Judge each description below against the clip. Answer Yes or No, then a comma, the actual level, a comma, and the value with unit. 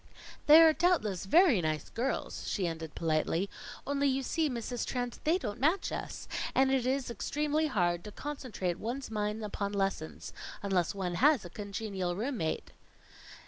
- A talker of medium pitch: No, high, 225 Hz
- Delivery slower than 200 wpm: Yes, average, 160 wpm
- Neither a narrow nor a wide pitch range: No, wide, 6.7 semitones